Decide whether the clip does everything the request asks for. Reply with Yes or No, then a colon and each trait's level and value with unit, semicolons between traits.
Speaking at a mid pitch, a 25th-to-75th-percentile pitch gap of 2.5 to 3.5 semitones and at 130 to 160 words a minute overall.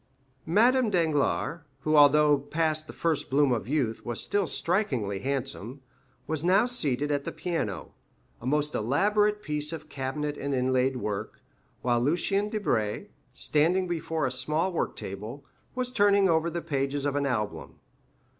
No: medium, 150 Hz; average, 4.7 semitones; average, 150 wpm